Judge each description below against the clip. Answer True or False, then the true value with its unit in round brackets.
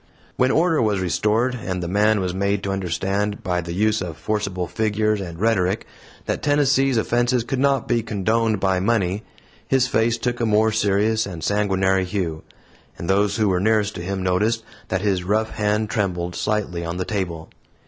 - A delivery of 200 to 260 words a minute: False (180 wpm)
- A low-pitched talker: True (105 Hz)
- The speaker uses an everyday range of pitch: True (3.2 semitones)